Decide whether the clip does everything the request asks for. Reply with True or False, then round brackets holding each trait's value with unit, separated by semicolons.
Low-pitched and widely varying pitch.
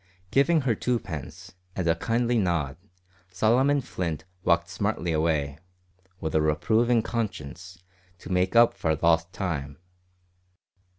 True (90 Hz; 6.5 semitones)